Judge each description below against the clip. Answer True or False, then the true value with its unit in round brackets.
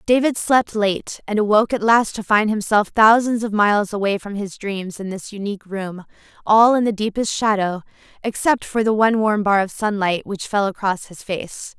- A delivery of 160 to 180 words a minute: False (200 wpm)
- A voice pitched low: False (210 Hz)